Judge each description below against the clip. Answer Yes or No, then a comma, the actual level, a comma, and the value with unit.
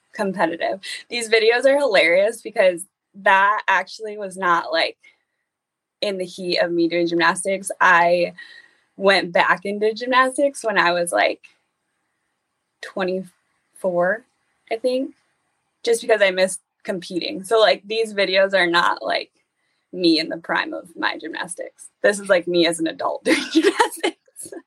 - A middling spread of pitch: No, wide, 7.3 semitones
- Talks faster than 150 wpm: No, average, 140 wpm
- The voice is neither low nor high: No, high, 200 Hz